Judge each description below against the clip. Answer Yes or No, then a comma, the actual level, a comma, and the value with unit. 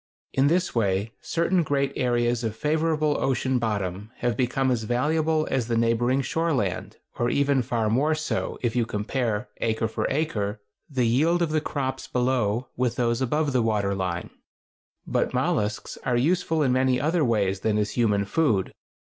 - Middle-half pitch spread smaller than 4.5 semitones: No, average, 4.8 semitones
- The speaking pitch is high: No, low, 125 Hz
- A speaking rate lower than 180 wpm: Yes, average, 170 wpm